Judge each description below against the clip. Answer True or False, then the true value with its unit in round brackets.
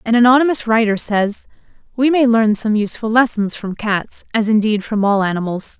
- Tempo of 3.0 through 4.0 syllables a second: False (5.3 syllables/s)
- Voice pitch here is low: False (220 Hz)